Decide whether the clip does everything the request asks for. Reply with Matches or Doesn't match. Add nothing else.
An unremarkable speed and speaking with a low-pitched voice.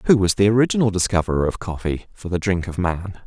Doesn't match